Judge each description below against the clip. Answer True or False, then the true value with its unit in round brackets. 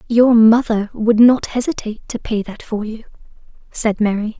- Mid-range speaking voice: False (220 Hz)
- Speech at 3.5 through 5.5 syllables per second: True (4.8 syllables/s)